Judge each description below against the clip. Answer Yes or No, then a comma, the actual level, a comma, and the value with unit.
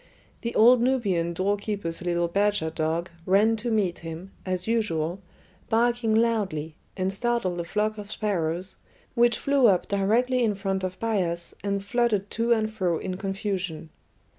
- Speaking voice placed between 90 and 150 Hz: No, high, 200 Hz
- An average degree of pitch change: Yes, average, 4.1 semitones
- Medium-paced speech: Yes, average, 150 wpm